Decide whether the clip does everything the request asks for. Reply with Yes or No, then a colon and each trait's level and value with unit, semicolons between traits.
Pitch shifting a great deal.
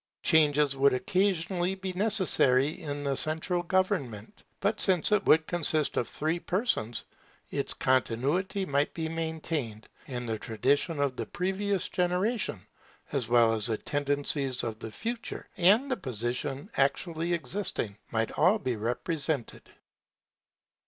Yes: wide, 6.1 semitones